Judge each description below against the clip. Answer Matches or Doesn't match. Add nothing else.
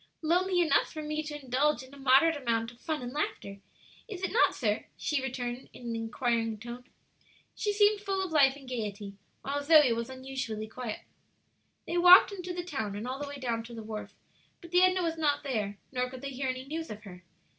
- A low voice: Doesn't match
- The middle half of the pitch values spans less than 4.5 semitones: Doesn't match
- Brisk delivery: Matches